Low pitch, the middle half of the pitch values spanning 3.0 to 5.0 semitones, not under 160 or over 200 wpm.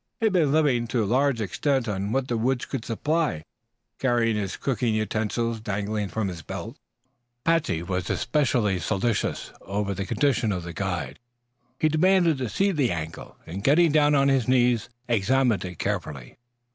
No: low, 115 Hz; wide, 5.6 semitones; average, 170 wpm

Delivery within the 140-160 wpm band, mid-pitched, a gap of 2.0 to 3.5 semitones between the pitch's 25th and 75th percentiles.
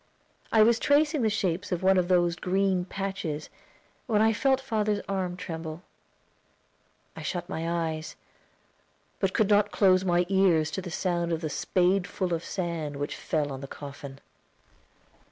Yes: average, 155 wpm; medium, 180 Hz; average, 3.2 semitones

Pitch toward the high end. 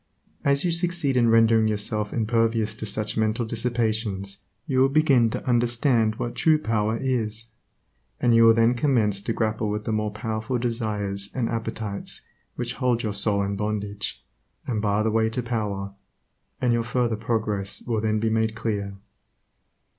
No: low, 110 Hz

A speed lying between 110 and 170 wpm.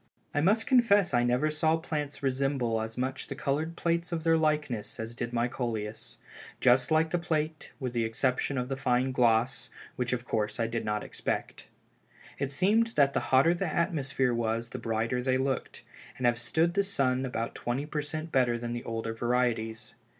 No: average, 190 wpm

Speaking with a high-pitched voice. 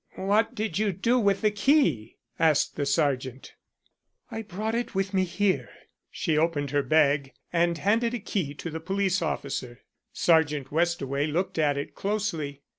No: medium, 170 Hz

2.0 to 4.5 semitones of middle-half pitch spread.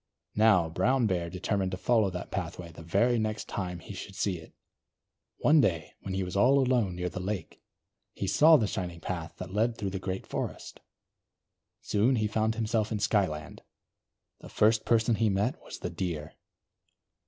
Yes: average, 3.7 semitones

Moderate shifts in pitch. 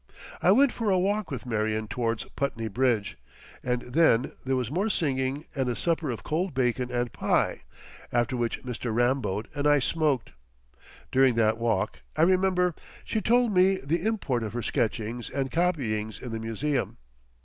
No: wide, 6.4 semitones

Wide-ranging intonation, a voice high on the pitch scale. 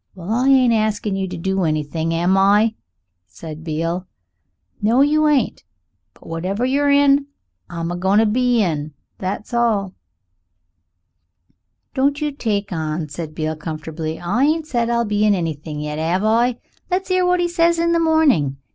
Yes: wide, 8.1 semitones; high, 205 Hz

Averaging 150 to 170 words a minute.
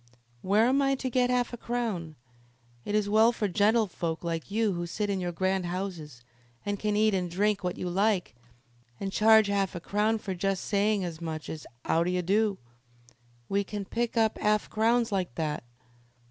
No: average, 190 wpm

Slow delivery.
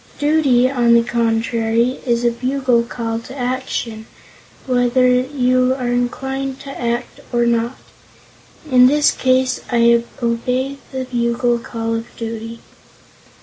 Yes: slow, 125 wpm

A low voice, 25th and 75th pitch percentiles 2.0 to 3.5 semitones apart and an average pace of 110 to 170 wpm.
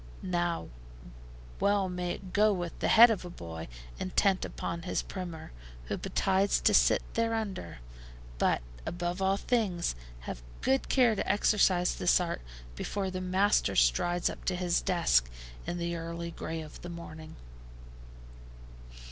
No: medium, 180 Hz; narrow, 2.6 semitones; average, 145 wpm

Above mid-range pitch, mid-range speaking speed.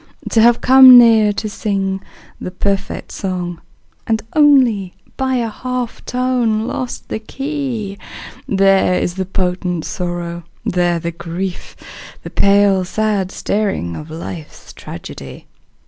No: high, 200 Hz; slow, 125 wpm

